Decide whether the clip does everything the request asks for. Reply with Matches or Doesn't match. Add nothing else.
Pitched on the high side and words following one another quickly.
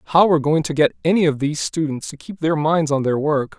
Doesn't match